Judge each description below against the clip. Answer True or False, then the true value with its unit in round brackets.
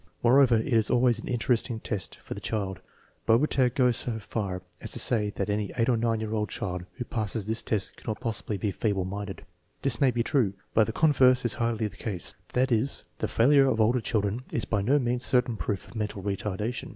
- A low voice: True (115 Hz)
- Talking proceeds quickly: True (210 wpm)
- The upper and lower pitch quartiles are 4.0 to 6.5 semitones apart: False (2.9 semitones)